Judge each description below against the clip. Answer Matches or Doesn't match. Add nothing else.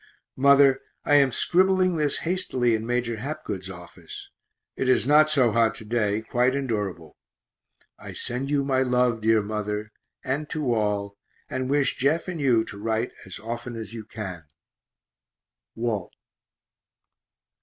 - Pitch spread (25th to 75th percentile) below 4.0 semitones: Doesn't match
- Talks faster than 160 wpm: Doesn't match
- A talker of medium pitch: Doesn't match